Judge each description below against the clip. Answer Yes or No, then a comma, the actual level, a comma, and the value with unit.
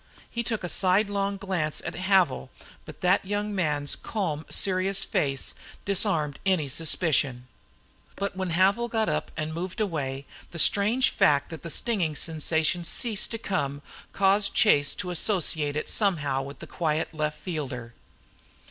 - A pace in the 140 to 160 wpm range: Yes, average, 150 wpm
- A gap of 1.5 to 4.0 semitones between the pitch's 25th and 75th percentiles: No, average, 4.8 semitones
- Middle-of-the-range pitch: Yes, medium, 175 Hz